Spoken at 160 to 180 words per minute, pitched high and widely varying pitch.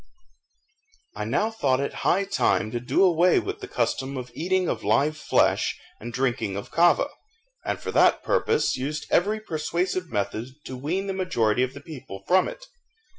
No: average, 170 wpm; medium, 155 Hz; wide, 6.8 semitones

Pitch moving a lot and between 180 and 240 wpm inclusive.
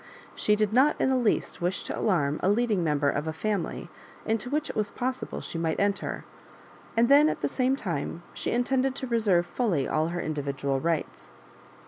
Yes: wide, 7.3 semitones; average, 190 wpm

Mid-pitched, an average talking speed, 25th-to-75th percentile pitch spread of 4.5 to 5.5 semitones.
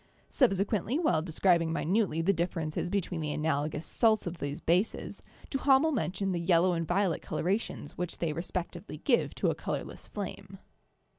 No: medium, 175 Hz; average, 160 wpm; average, 3.6 semitones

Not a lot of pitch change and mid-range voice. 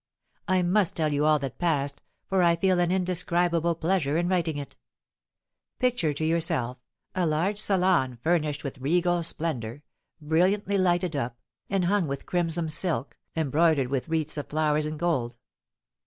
No: average, 3.2 semitones; medium, 165 Hz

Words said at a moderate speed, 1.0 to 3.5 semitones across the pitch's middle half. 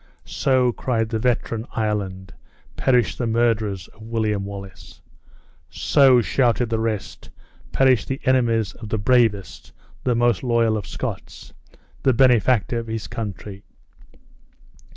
No: slow, 125 wpm; average, 2.7 semitones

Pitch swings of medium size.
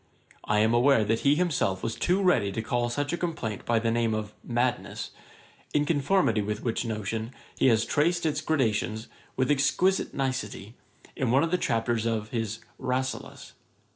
Yes: average, 4.6 semitones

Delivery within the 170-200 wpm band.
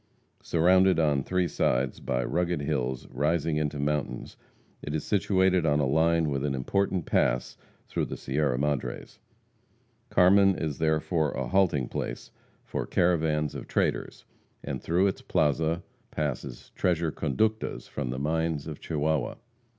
No: average, 140 wpm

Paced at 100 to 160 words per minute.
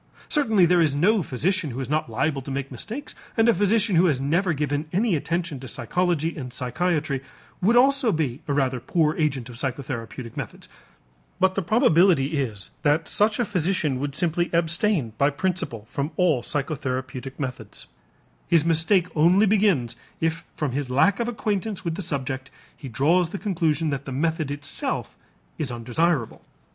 No: average, 170 wpm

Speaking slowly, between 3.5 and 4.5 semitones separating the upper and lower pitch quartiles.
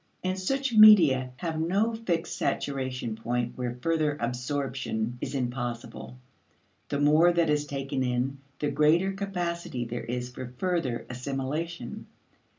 No: slow, 130 wpm; wide, 5.5 semitones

